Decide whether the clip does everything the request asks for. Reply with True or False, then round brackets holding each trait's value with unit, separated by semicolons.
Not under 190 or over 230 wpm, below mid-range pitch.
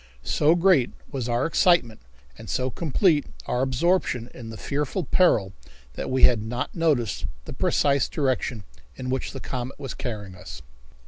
False (155 wpm; 130 Hz)